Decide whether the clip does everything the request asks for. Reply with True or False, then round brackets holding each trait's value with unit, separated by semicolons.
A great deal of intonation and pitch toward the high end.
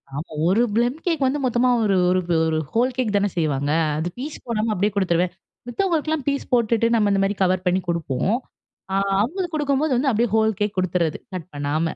True (6.1 semitones; 215 Hz)